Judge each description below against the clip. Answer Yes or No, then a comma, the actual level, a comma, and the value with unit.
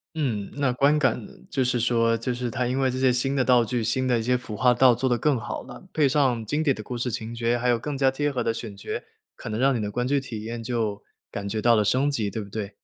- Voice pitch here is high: No, low, 125 Hz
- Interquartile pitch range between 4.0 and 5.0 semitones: No, narrow, 2.6 semitones